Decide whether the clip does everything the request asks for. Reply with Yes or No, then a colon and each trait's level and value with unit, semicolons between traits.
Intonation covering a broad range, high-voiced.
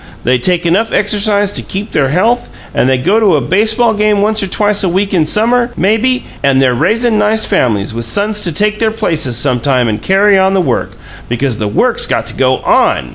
Yes: wide, 8.2 semitones; high, 195 Hz